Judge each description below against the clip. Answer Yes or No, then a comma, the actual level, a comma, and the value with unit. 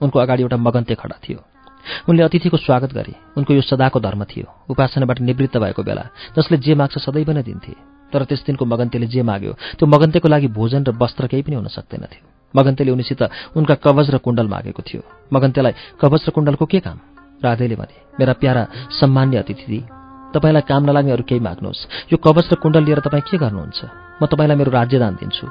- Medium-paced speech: Yes, average, 190 wpm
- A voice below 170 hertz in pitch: Yes, low, 135 Hz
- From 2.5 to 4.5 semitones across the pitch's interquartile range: Yes, average, 3.5 semitones